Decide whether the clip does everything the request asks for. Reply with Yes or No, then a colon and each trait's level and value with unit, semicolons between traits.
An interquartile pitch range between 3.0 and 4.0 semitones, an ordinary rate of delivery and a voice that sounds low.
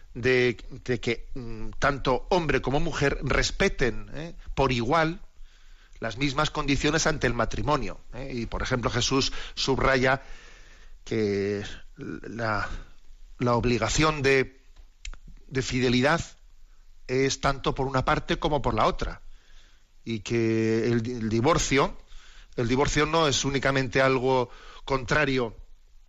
No: average, 3.3 semitones; slow, 120 wpm; low, 130 Hz